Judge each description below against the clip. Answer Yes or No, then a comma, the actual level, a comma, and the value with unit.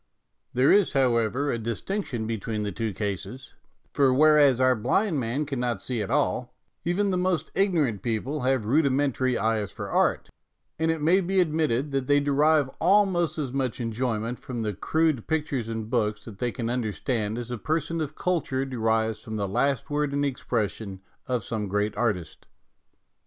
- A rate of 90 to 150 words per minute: No, average, 180 wpm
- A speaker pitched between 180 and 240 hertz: No, low, 130 Hz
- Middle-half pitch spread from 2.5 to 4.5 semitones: No, average, 5.1 semitones